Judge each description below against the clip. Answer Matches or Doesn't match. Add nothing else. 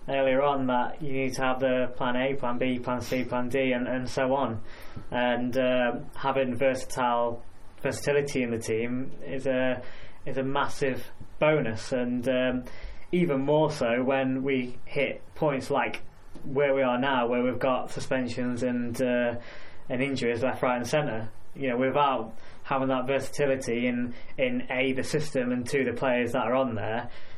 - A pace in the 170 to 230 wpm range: Matches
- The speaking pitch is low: Matches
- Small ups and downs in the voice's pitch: Matches